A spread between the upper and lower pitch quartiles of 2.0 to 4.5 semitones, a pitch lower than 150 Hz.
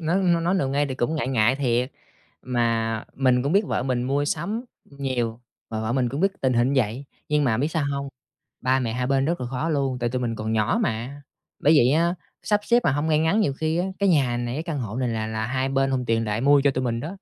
Yes: average, 4.0 semitones; low, 135 Hz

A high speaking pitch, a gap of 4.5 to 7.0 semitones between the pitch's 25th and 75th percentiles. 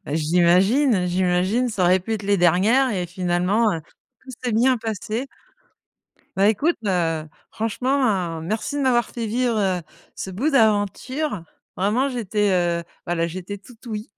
Yes: high, 205 Hz; average, 5.0 semitones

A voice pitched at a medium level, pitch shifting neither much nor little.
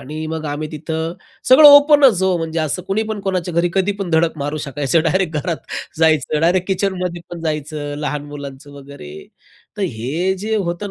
Yes: medium, 165 Hz; average, 4.1 semitones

